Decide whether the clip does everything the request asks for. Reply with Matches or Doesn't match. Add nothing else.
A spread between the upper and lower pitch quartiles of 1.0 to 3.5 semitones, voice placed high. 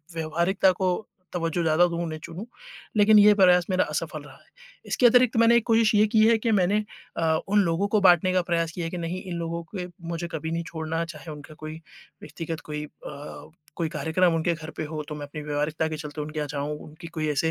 Doesn't match